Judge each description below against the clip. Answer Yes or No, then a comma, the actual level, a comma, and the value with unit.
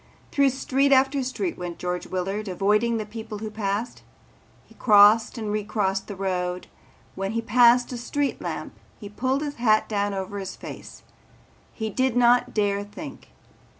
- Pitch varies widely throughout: No, average, 3.6 semitones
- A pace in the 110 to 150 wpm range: No, average, 160 wpm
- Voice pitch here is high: Yes, high, 215 Hz